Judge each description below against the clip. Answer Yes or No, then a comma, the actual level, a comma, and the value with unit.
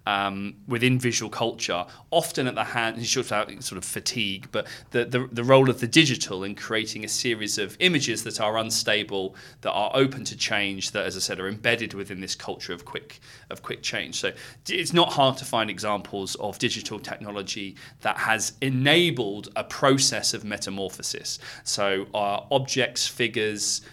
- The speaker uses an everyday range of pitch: Yes, average, 3.9 semitones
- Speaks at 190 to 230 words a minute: No, average, 170 wpm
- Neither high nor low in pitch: No, low, 110 Hz